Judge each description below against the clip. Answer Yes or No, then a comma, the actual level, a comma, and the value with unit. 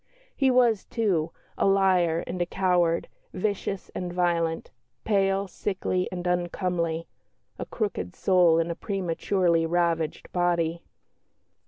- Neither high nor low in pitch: Yes, medium, 180 Hz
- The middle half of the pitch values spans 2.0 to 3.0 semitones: Yes, narrow, 2.5 semitones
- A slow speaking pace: Yes, slow, 120 wpm